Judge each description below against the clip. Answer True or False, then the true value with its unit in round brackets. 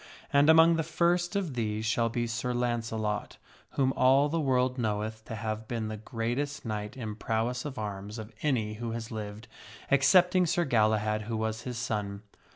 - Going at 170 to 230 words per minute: True (175 wpm)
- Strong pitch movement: False (3.9 semitones)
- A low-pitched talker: True (115 Hz)